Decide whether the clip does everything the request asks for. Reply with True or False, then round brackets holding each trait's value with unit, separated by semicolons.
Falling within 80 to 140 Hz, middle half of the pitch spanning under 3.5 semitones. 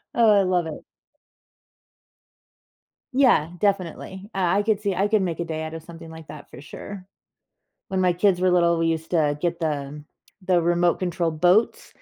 False (175 Hz; 2.9 semitones)